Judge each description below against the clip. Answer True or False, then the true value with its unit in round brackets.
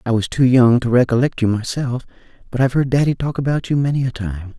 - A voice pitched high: False (125 Hz)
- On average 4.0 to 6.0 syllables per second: False (6.2 syllables/s)